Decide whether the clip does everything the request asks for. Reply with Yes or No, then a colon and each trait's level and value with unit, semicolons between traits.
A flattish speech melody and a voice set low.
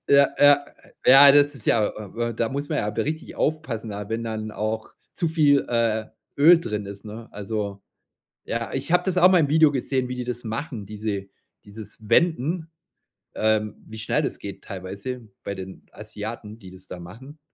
No: average, 5.2 semitones; low, 115 Hz